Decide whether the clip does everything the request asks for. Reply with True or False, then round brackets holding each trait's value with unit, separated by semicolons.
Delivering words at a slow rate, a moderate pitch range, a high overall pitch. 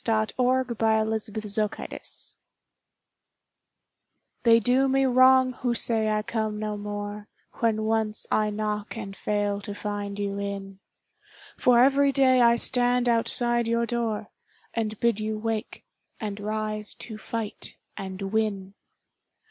False (120 wpm; 2.2 semitones; 220 Hz)